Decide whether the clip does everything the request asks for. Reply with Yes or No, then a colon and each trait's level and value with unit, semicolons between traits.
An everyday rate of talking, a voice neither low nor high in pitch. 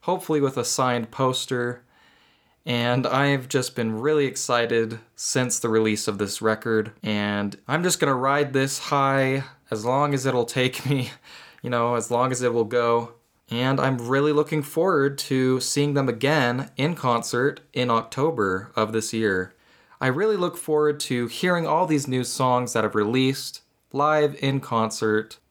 No: average, 165 wpm; low, 125 Hz